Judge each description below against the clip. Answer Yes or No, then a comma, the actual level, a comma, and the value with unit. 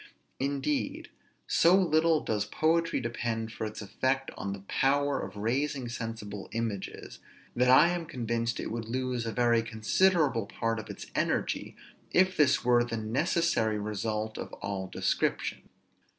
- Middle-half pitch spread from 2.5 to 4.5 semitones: No, average, 5.2 semitones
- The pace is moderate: Yes, average, 145 wpm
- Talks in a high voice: No, low, 120 Hz